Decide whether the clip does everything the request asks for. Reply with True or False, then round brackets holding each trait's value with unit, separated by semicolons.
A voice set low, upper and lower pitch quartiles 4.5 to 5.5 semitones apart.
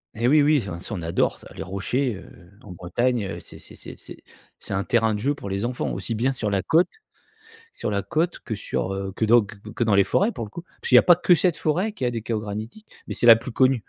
True (115 Hz; 5.2 semitones)